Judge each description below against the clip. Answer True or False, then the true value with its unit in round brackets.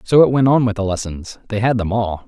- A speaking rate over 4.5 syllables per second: True (5.8 syllables/s)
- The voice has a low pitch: True (110 Hz)